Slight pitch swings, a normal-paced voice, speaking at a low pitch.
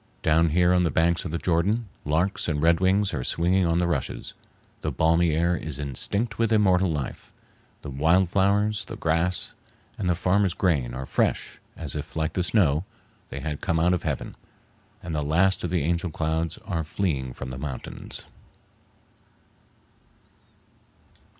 No: average, 3.2 semitones; average, 165 wpm; very low, 85 Hz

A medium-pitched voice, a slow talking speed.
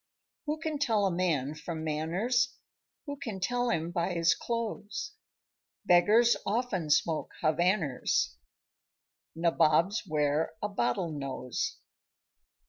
Yes: medium, 175 Hz; slow, 110 wpm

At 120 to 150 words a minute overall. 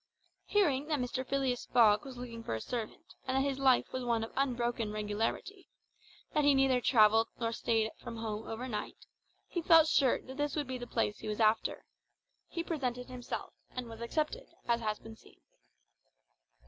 No: average, 180 wpm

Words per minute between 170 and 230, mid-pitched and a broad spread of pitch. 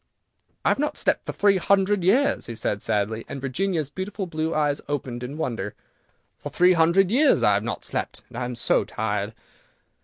Yes: average, 190 wpm; medium, 155 Hz; wide, 8.1 semitones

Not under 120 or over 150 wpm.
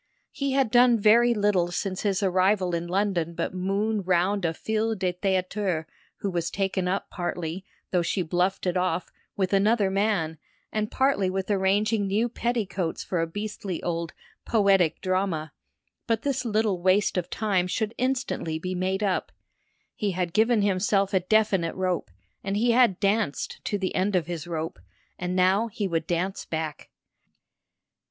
No: average, 160 wpm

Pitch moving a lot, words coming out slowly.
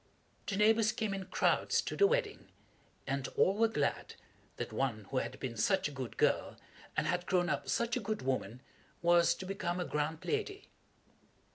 No: wide, 7.3 semitones; average, 180 wpm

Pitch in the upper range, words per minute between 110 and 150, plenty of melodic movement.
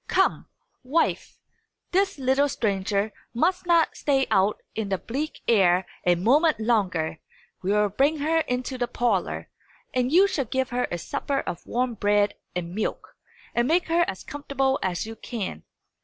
No: high, 245 Hz; average, 160 wpm; wide, 6.0 semitones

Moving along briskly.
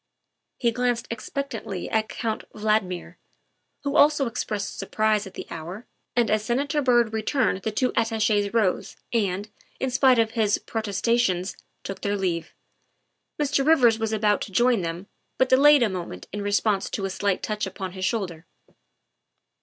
No: average, 160 wpm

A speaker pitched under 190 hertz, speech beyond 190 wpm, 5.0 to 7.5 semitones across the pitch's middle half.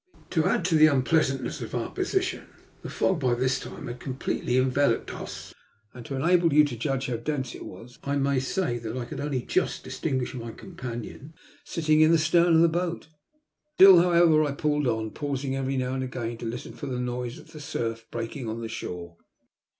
No: low, 135 Hz; fast, 205 wpm; average, 4.2 semitones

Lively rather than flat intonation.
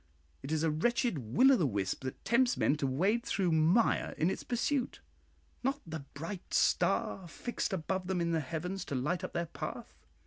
Yes: wide, 6.5 semitones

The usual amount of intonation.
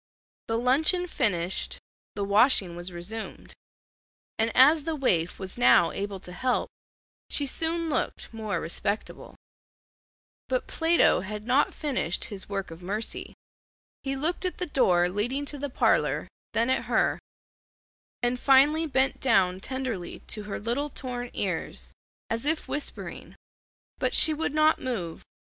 No: wide, 6.6 semitones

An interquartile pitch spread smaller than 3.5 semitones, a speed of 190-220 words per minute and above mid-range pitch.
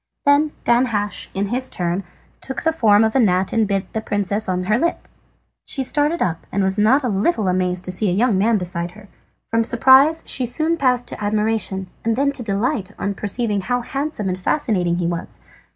No: average, 4.8 semitones; average, 200 wpm; high, 215 Hz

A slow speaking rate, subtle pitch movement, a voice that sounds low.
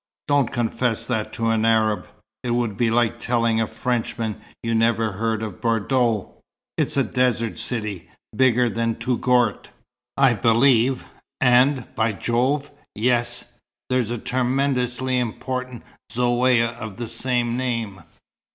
Yes: slow, 130 wpm; narrow, 1.9 semitones; low, 120 Hz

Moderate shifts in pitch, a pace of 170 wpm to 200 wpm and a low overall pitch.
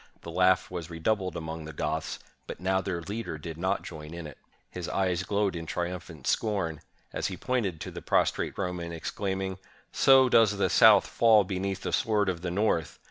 Yes: average, 3.2 semitones; average, 190 wpm; very low, 90 Hz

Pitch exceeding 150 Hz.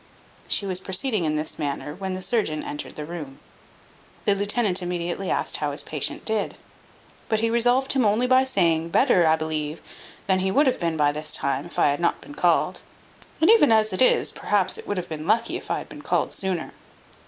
Yes: medium, 185 Hz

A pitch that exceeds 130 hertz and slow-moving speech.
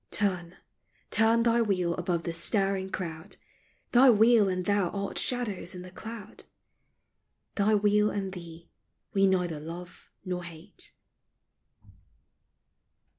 Yes: high, 190 Hz; slow, 120 wpm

